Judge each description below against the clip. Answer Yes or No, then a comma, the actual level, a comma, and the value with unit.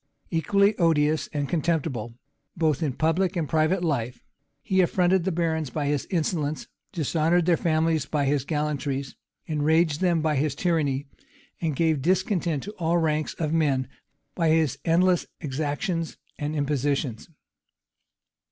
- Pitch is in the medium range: Yes, medium, 155 Hz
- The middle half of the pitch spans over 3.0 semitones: No, average, 2.7 semitones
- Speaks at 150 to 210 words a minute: No, slow, 135 wpm